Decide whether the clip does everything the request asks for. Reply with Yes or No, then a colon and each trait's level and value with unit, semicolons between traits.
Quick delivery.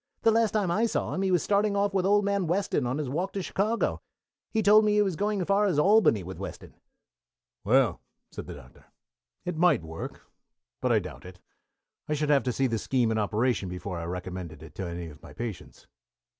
Yes: fast, 220 wpm